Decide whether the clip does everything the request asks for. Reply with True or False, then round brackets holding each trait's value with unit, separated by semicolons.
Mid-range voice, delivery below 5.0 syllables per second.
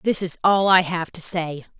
True (175 Hz; 4.6 syllables/s)